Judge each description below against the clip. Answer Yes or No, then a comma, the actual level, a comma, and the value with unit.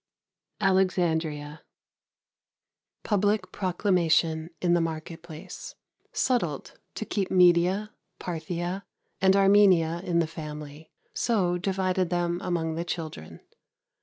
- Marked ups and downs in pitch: No, average, 2.8 semitones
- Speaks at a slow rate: Yes, slow, 100 wpm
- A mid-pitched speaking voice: Yes, medium, 175 Hz